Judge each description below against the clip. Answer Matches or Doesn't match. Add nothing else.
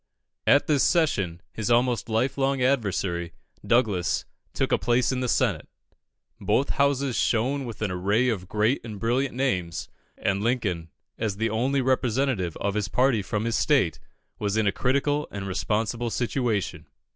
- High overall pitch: Doesn't match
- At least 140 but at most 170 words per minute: Matches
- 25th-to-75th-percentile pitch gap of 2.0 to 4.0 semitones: Doesn't match